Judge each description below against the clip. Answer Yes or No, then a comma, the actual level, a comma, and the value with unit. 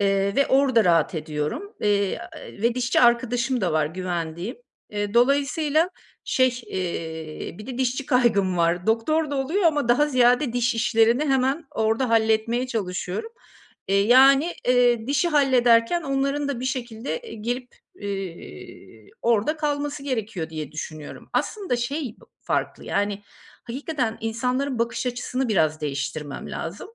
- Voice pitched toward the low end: No, high, 235 Hz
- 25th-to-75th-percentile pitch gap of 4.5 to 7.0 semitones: Yes, average, 5.3 semitones